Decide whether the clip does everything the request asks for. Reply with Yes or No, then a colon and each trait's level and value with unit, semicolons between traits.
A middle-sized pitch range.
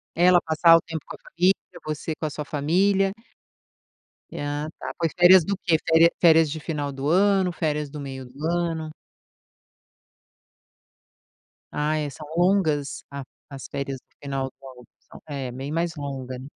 Yes: average, 3.3 semitones